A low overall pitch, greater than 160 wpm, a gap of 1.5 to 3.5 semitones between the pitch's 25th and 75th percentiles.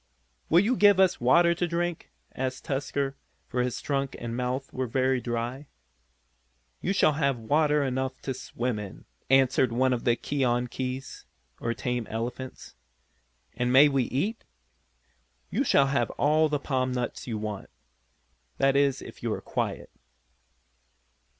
No: low, 130 Hz; average, 145 wpm; average, 2.8 semitones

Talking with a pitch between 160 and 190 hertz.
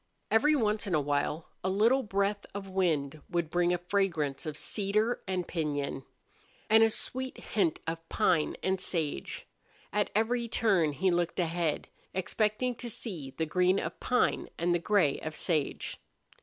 Yes: medium, 185 Hz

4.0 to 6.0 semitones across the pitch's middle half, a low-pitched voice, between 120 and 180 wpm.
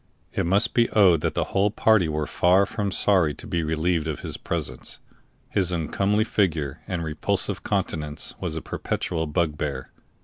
Yes: average, 4.3 semitones; very low, 85 Hz; average, 165 wpm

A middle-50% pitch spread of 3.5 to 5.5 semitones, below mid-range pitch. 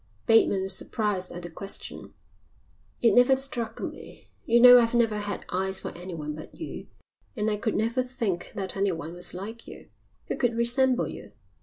No: average, 4.0 semitones; high, 215 Hz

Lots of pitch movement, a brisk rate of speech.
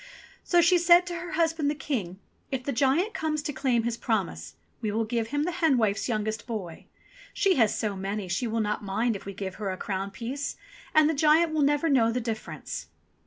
Yes: wide, 6.5 semitones; fast, 215 wpm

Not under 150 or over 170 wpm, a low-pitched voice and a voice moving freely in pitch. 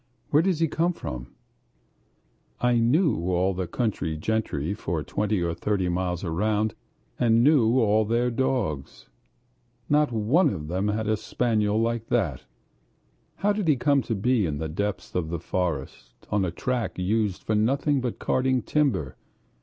Yes: average, 160 wpm; low, 110 Hz; wide, 5.8 semitones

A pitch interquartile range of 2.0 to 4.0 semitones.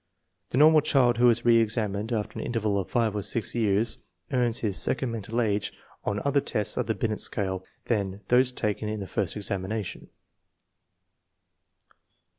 Yes: average, 2.9 semitones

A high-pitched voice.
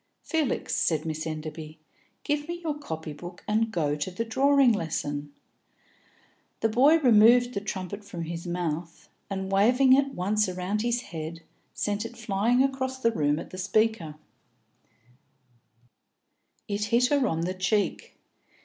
Yes: high, 205 Hz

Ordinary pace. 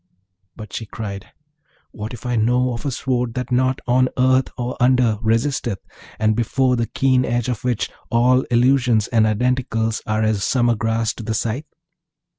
Yes: average, 170 wpm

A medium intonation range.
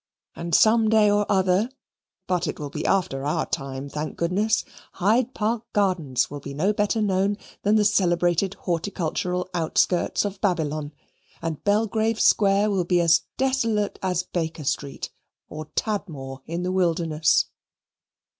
Yes: average, 4.3 semitones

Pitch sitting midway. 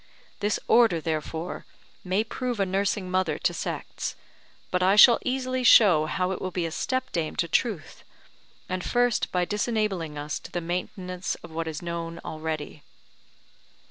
Yes: medium, 180 Hz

